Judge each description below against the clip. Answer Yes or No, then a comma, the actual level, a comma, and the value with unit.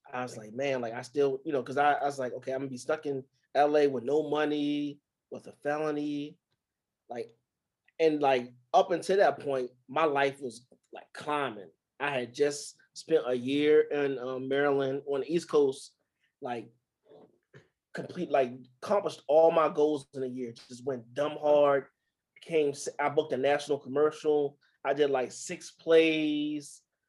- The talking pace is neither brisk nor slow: Yes, average, 170 wpm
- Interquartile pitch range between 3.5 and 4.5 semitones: No, narrow, 2.4 semitones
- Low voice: No, medium, 145 Hz